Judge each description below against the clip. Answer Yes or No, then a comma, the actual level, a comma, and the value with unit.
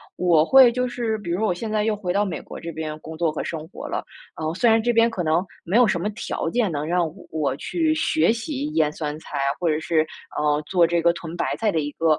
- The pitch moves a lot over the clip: Yes, wide, 5.9 semitones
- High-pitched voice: No, medium, 175 Hz